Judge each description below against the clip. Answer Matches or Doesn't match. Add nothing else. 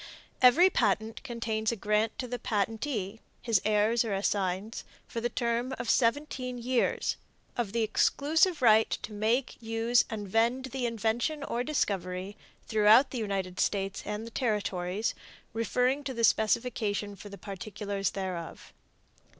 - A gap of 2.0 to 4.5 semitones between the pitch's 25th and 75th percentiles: Matches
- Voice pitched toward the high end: Matches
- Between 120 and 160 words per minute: Matches